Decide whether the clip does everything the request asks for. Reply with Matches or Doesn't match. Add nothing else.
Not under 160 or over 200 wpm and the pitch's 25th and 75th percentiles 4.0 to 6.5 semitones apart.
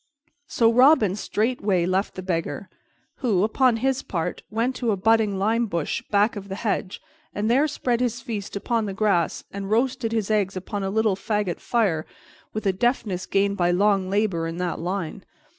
Doesn't match